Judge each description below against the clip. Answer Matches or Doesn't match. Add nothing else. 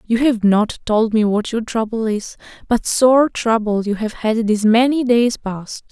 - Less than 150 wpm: Doesn't match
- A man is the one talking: Doesn't match